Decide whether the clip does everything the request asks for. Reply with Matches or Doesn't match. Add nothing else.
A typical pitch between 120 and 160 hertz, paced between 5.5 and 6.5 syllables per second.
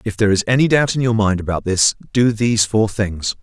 Doesn't match